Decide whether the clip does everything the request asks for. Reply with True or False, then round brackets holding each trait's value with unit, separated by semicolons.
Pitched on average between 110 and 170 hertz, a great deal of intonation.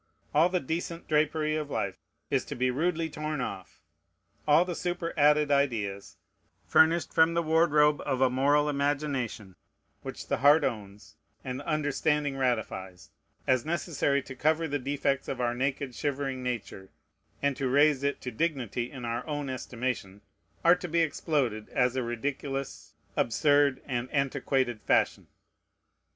False (140 Hz; 3.4 semitones)